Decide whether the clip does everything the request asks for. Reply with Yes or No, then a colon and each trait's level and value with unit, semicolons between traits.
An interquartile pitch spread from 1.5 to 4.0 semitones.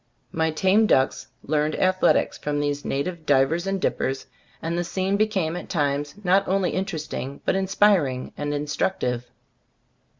No: average, 4.6 semitones